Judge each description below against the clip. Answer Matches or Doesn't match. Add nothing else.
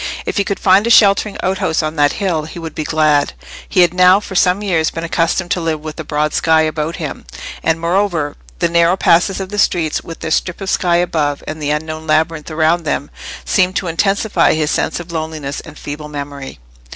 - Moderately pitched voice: Matches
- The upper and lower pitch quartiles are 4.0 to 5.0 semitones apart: Doesn't match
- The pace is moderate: Doesn't match